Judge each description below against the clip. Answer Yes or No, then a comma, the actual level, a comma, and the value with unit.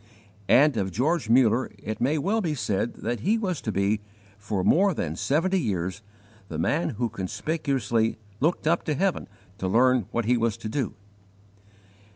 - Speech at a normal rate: Yes, average, 170 wpm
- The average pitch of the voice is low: Yes, low, 120 Hz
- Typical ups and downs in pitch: No, wide, 6.7 semitones